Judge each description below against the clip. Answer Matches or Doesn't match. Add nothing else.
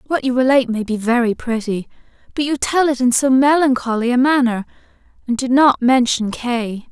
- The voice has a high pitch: Matches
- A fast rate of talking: Doesn't match